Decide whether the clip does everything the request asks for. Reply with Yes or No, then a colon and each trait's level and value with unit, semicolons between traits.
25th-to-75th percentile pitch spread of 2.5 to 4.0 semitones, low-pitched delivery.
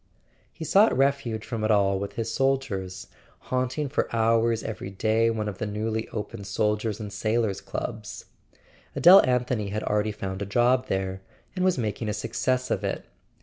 Yes: average, 3.4 semitones; low, 110 Hz